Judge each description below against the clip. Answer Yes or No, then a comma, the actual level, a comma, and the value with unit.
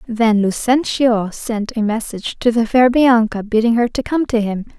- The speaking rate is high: No, average, 190 wpm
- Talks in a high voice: Yes, high, 230 Hz